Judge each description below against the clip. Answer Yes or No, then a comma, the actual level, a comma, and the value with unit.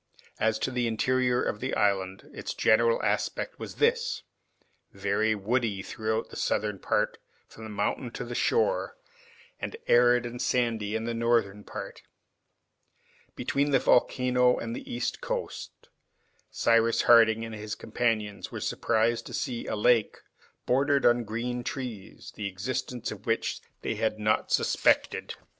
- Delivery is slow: No, average, 145 wpm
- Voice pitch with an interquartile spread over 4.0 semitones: No, narrow, 2.4 semitones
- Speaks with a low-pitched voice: Yes, low, 115 Hz